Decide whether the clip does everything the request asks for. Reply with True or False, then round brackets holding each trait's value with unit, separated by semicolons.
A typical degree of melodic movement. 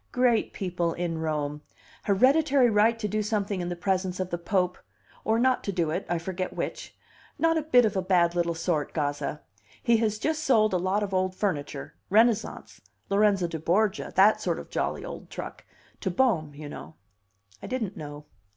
True (4.3 semitones)